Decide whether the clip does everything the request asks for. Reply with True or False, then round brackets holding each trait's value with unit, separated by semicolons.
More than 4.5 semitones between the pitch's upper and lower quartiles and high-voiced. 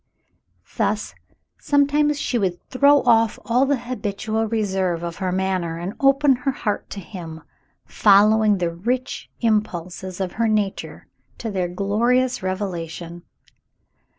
True (5.0 semitones; 210 Hz)